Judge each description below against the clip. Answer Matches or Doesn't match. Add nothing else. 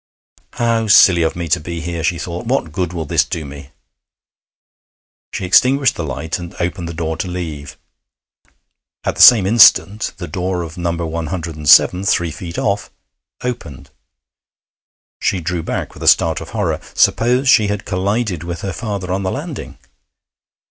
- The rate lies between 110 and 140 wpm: Doesn't match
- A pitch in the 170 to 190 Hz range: Doesn't match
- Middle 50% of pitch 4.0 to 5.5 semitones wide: Doesn't match